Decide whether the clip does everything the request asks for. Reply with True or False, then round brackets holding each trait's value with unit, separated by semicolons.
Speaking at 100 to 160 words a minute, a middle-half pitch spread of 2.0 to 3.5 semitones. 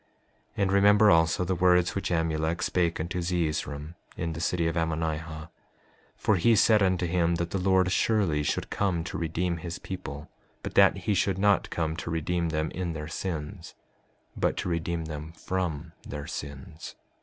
False (175 wpm; 2.4 semitones)